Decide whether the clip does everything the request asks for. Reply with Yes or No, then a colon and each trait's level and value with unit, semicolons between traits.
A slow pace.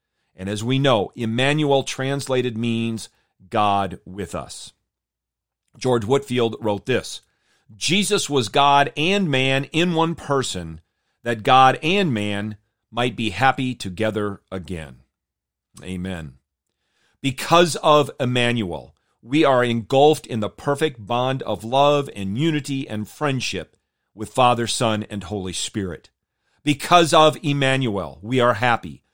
Yes: slow, 125 wpm